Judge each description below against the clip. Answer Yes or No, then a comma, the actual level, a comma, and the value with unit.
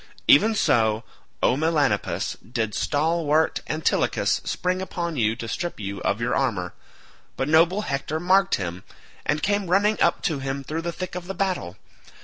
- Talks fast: No, average, 160 wpm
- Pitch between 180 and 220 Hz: No, medium, 155 Hz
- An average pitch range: No, wide, 7.5 semitones